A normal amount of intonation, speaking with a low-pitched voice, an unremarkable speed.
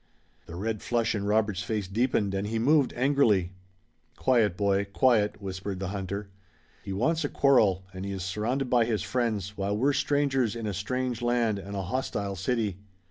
Yes: average, 3.9 semitones; low, 105 Hz; average, 180 wpm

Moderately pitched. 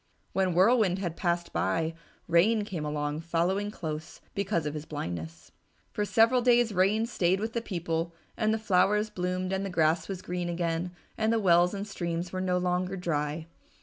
Yes: medium, 180 Hz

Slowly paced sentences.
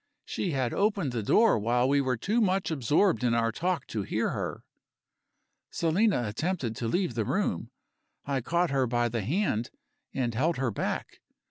No: average, 170 wpm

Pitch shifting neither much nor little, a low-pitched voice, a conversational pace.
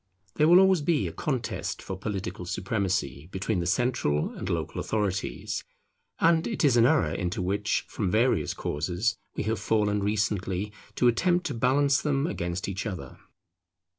No: wide, 5.8 semitones; low, 105 Hz; average, 160 wpm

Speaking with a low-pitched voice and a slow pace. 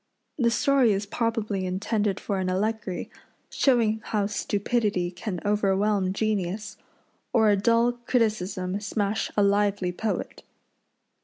No: high, 205 Hz; slow, 115 wpm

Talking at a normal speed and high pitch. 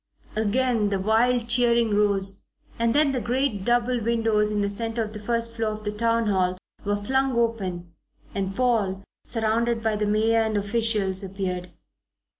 Yes: average, 165 wpm; high, 220 Hz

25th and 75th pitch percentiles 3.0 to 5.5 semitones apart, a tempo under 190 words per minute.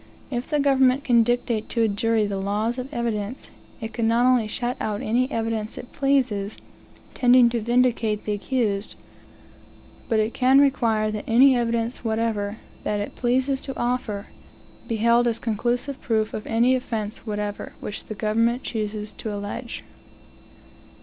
No: narrow, 2.6 semitones; average, 155 wpm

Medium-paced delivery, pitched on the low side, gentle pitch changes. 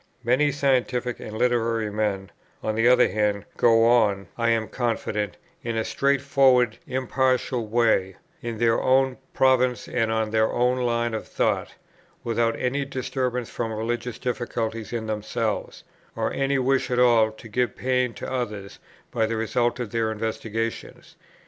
Yes: average, 150 wpm; low, 120 Hz; narrow, 2.3 semitones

